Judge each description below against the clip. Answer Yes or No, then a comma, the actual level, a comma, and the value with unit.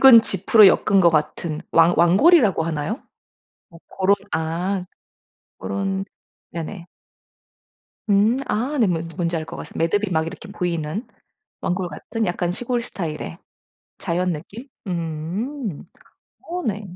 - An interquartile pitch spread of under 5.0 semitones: Yes, average, 4.3 semitones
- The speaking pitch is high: No, medium, 180 Hz